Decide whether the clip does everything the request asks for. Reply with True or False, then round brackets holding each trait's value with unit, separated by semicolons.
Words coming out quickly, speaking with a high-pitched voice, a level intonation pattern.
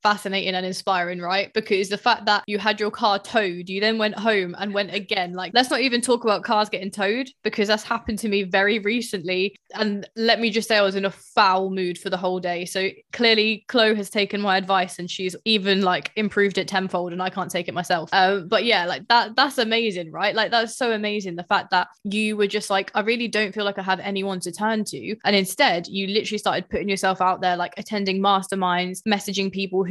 True (230 wpm; 200 Hz; 2.3 semitones)